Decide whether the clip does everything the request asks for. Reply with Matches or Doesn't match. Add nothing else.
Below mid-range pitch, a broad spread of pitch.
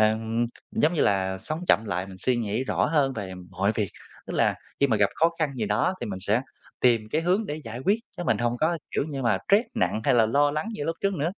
Matches